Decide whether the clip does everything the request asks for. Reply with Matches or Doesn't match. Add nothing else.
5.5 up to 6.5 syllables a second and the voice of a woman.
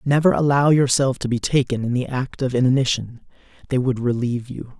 Doesn't match